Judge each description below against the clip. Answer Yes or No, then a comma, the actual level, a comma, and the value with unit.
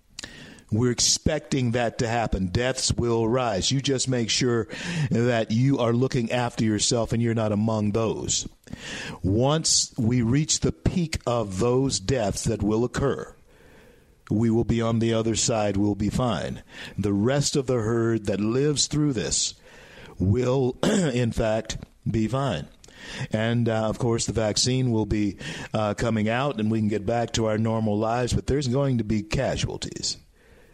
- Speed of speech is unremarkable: Yes, average, 165 wpm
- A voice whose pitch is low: Yes, low, 115 Hz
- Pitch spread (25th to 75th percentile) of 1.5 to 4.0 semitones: Yes, average, 2.9 semitones